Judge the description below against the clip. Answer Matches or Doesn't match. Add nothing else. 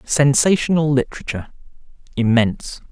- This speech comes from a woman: Doesn't match